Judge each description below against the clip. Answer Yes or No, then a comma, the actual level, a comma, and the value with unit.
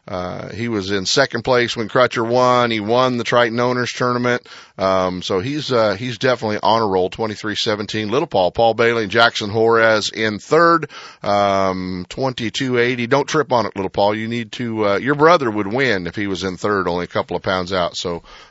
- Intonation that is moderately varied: Yes, average, 3.4 semitones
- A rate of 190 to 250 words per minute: Yes, average, 200 wpm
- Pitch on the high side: No, low, 115 Hz